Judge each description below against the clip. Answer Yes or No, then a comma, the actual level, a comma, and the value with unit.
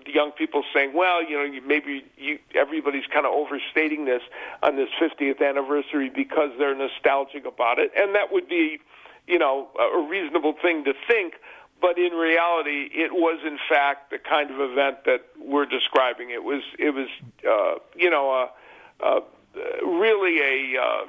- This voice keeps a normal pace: Yes, average, 175 wpm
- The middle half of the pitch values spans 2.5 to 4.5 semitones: Yes, average, 4.1 semitones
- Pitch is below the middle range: No, medium, 150 Hz